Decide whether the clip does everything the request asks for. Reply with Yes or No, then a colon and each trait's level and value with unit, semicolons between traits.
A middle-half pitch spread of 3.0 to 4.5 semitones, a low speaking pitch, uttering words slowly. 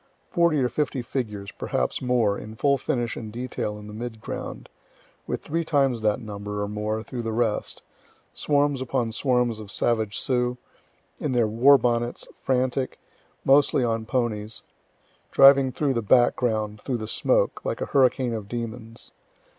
No: average, 3.3 semitones; low, 120 Hz; average, 155 wpm